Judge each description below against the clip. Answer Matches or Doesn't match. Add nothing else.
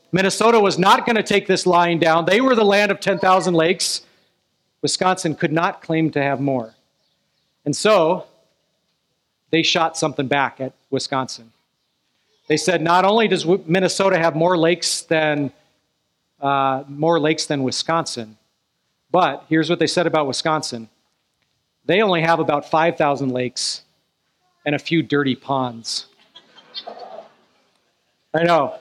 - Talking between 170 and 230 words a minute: Doesn't match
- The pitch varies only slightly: Doesn't match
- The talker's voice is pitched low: Doesn't match